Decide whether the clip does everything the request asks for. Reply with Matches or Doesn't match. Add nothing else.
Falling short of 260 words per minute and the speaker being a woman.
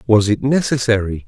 Doesn't match